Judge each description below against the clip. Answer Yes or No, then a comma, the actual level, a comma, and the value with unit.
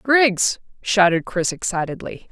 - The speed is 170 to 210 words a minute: No, slow, 105 wpm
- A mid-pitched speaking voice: No, high, 200 Hz